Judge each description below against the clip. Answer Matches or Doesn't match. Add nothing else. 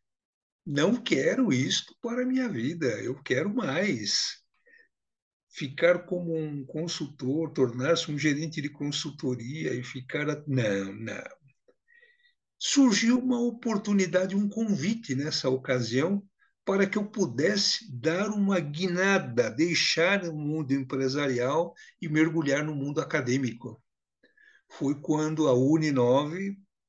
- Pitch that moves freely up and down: Matches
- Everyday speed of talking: Doesn't match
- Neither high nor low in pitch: Matches